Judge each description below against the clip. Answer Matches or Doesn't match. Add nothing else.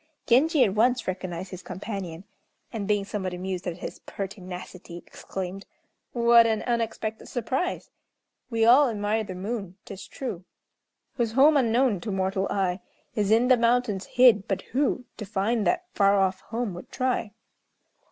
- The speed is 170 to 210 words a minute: Doesn't match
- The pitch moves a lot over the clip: Doesn't match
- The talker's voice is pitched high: Matches